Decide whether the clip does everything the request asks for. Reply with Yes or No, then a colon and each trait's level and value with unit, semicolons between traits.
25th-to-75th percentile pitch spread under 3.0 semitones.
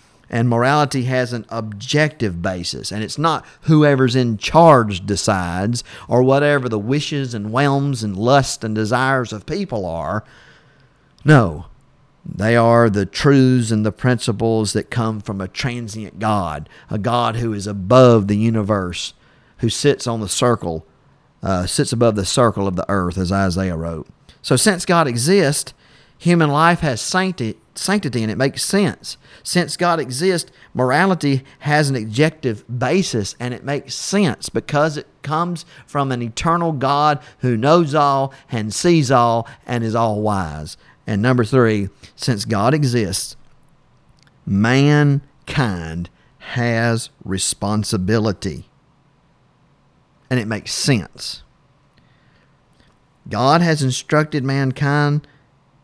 No: average, 5.0 semitones